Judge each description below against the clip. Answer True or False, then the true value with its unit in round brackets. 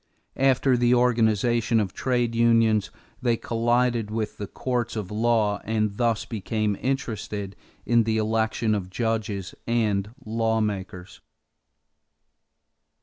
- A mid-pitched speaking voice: False (110 Hz)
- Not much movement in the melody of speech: True (2.0 semitones)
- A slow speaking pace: True (110 wpm)